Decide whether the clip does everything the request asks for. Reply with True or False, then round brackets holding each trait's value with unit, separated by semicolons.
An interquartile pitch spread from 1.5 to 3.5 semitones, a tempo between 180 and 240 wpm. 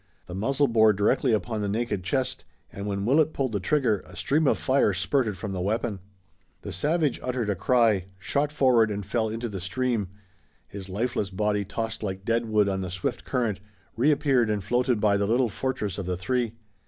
False (4.2 semitones; 195 wpm)